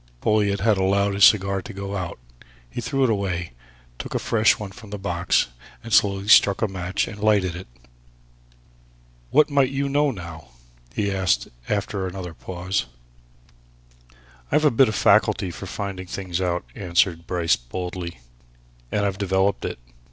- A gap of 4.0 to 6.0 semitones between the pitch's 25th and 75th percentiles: No, narrow, 2.6 semitones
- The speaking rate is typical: Yes, average, 160 wpm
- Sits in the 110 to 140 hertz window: No, low, 100 Hz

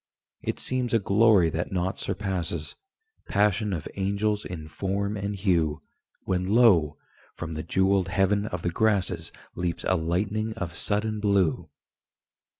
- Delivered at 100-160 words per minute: Yes, average, 140 wpm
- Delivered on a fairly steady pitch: No, average, 3.2 semitones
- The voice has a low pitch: Yes, very low, 95 Hz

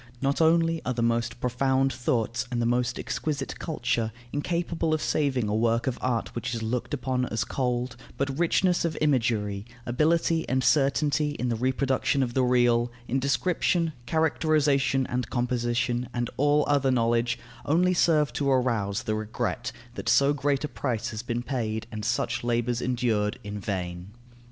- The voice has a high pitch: No, low, 125 Hz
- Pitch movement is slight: No, average, 3.5 semitones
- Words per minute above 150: Yes, average, 165 wpm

